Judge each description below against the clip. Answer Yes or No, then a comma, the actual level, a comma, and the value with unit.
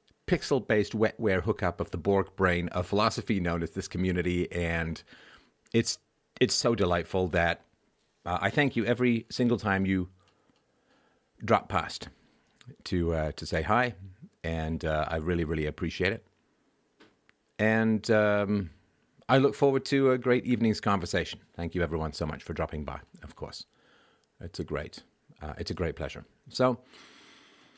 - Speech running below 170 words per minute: Yes, average, 150 wpm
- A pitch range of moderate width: Yes, average, 5.0 semitones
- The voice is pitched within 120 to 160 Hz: No, very low, 95 Hz